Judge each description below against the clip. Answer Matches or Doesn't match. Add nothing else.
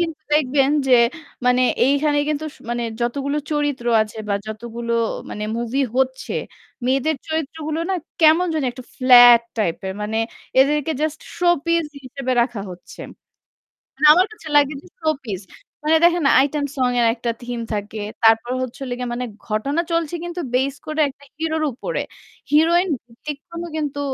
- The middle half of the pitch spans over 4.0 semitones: Matches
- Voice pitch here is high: Matches